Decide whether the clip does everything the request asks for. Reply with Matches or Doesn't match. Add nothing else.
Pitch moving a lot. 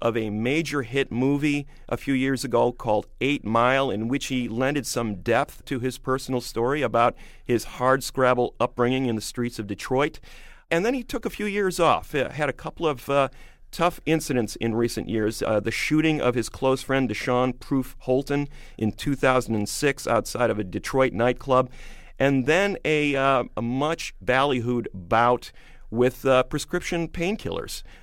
Doesn't match